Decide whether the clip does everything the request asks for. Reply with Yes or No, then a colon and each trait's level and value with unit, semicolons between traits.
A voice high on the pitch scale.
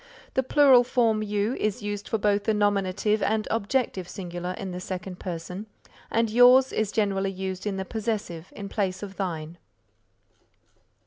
Yes: high, 205 Hz